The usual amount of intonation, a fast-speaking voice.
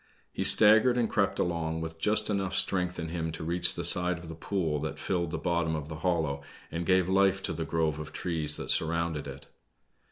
No: narrow, 2.3 semitones; fast, 215 wpm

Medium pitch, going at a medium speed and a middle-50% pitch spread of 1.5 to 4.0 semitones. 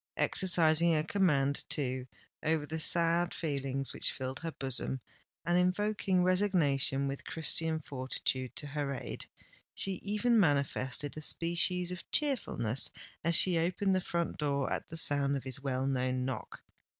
No: medium, 155 Hz; average, 150 wpm; average, 4.5 semitones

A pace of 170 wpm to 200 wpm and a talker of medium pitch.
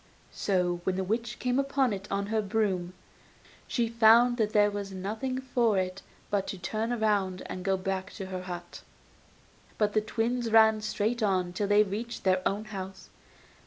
No: average, 180 wpm; high, 205 Hz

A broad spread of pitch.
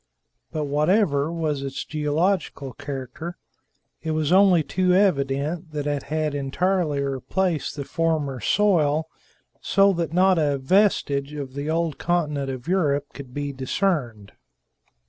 No: average, 3.8 semitones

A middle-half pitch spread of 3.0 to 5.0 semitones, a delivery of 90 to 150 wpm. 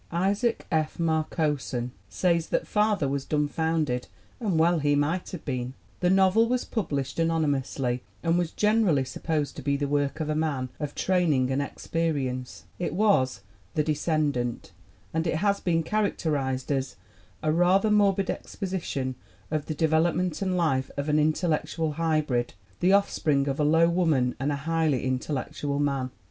No: average, 3.8 semitones; average, 165 wpm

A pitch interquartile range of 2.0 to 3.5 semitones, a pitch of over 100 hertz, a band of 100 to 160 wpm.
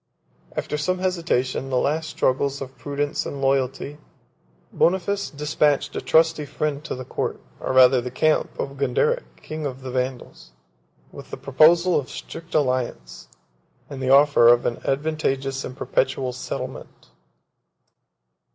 Yes: average, 3.1 semitones; medium, 140 Hz; average, 145 wpm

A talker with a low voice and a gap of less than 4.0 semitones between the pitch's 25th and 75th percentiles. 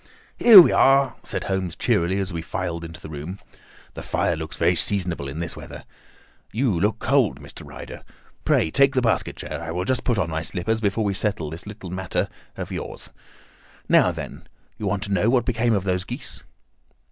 No: very low, 95 Hz; average, 5.0 semitones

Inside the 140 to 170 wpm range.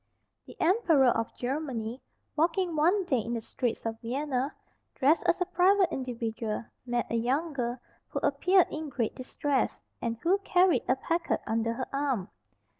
Yes: average, 160 wpm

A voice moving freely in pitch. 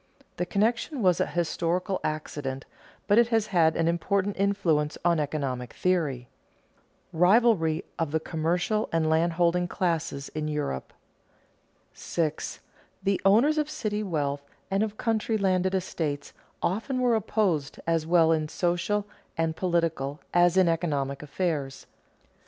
No: average, 4.2 semitones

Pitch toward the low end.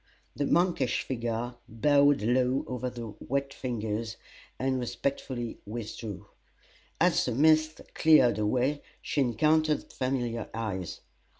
Yes: low, 125 Hz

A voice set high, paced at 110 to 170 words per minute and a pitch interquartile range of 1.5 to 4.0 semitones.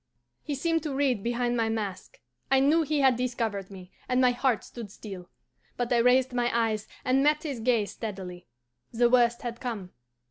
No: high, 240 Hz; average, 185 wpm; average, 3.3 semitones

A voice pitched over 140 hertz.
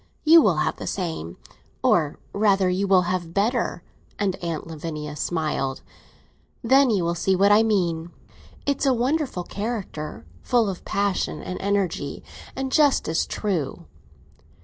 Yes: high, 190 Hz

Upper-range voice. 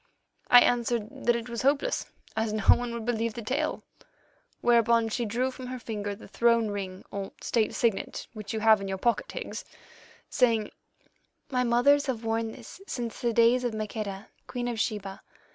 Yes: high, 230 Hz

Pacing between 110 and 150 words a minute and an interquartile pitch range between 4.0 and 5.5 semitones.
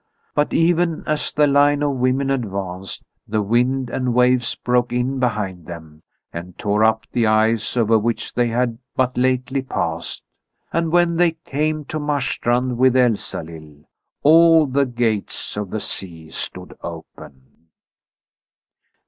Yes: average, 140 wpm; average, 4.9 semitones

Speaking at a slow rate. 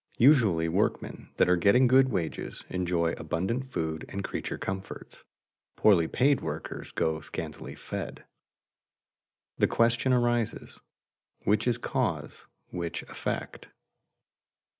Yes: slow, 115 wpm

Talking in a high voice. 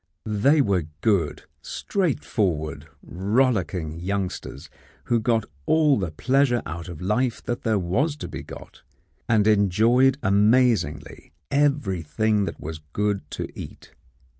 No: low, 105 Hz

